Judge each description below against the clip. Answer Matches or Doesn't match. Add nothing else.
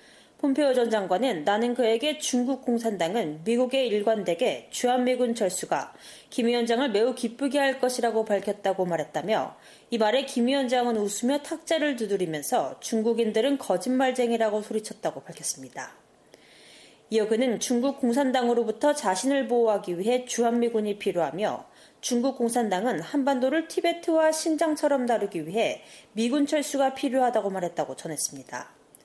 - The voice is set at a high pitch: Matches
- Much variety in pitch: Doesn't match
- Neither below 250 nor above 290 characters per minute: Doesn't match